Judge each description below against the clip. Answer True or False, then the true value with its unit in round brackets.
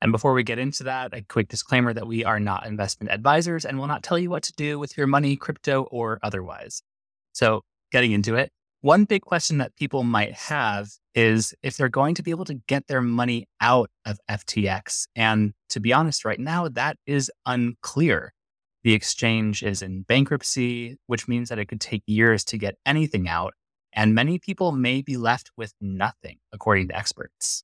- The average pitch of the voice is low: True (120 Hz)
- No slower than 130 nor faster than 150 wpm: False (195 wpm)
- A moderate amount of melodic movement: True (4.8 semitones)